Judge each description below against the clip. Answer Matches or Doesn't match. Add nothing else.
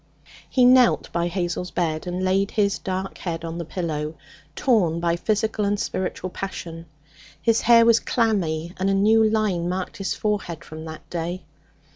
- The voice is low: Doesn't match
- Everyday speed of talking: Matches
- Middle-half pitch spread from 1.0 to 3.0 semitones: Doesn't match